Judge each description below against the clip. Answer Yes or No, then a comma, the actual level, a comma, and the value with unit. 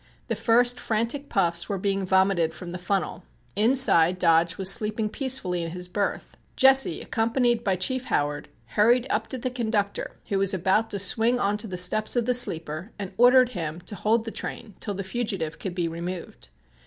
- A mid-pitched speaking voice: No, high, 200 Hz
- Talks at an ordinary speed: Yes, average, 190 wpm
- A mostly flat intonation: No, average, 4.5 semitones